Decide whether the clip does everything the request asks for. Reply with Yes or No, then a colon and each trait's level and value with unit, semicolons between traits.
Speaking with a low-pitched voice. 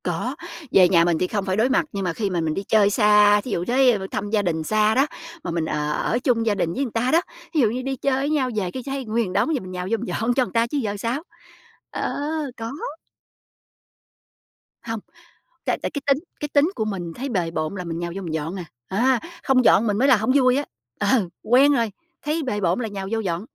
No: high, 215 Hz